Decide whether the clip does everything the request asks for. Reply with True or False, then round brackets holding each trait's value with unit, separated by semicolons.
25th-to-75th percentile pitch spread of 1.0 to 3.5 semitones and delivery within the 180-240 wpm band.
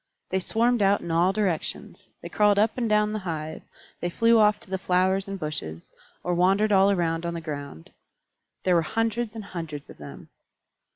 False (4.3 semitones; 190 wpm)